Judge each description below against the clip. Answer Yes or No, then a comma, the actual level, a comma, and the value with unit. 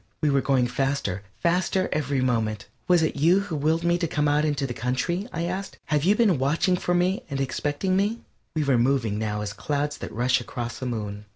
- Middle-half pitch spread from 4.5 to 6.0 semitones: Yes, wide, 5.5 semitones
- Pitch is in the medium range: Yes, medium, 145 Hz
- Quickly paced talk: Yes, fast, 215 wpm